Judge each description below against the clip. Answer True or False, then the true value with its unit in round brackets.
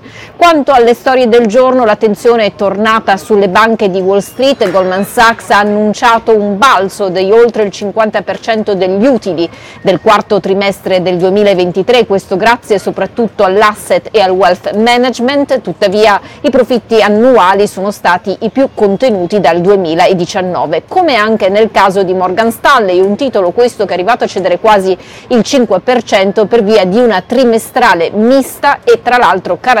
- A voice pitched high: True (210 Hz)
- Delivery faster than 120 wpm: True (155 wpm)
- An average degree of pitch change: True (3.7 semitones)